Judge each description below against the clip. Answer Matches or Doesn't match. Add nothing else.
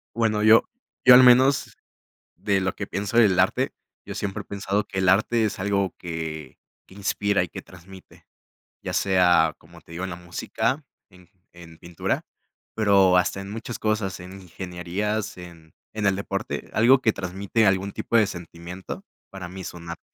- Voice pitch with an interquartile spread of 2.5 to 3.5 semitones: Matches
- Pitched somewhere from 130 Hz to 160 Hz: Doesn't match